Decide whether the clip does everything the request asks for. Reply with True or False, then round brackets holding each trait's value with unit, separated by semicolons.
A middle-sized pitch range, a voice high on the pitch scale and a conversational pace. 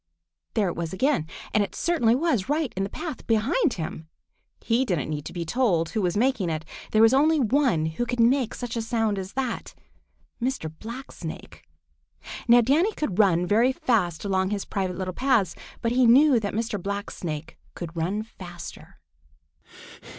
False (5.9 semitones; 220 Hz; 170 wpm)